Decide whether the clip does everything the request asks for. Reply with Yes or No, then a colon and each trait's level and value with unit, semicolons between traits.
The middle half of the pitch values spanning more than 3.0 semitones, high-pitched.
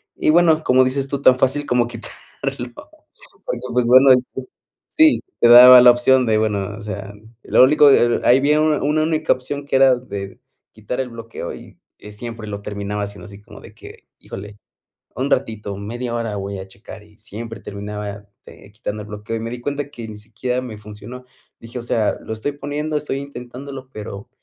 No: average, 4.2 semitones; low, 120 Hz